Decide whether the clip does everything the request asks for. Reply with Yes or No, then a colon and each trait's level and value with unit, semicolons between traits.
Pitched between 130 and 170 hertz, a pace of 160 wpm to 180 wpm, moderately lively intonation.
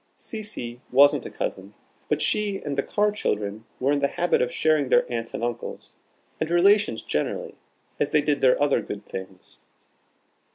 No: medium, 140 Hz; average, 170 wpm; wide, 6.7 semitones